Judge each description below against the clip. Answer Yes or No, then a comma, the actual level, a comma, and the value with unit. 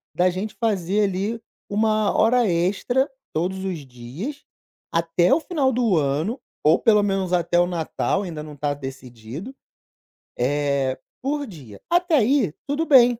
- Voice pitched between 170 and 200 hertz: Yes, high, 190 Hz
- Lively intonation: Yes, wide, 7.4 semitones